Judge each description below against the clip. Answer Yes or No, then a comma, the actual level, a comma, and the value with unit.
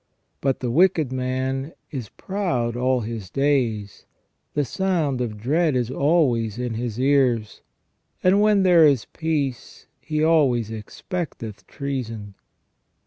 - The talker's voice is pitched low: Yes, low, 130 Hz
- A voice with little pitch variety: No, average, 5.0 semitones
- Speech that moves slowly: Yes, slow, 125 wpm